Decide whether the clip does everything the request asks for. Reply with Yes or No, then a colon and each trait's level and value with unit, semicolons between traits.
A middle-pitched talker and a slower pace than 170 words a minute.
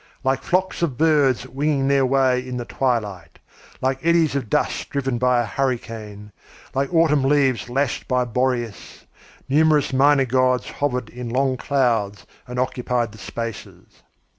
No: low, 130 Hz; average, 145 wpm